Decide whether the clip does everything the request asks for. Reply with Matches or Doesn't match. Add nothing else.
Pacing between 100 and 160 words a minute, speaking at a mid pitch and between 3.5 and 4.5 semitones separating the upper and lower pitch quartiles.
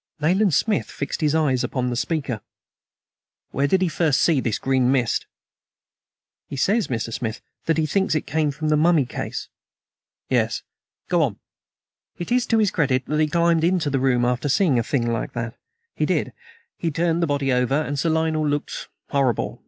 Doesn't match